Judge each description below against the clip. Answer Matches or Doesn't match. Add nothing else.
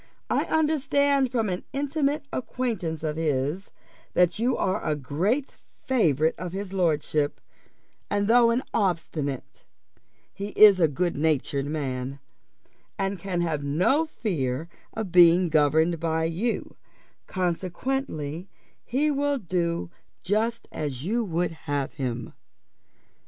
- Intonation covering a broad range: Matches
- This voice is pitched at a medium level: Matches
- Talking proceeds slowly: Matches